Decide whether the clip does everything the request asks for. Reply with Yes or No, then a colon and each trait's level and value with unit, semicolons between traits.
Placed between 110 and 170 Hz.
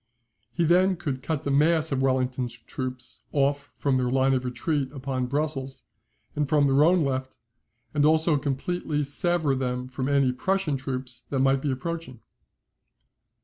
Yes: low, 135 Hz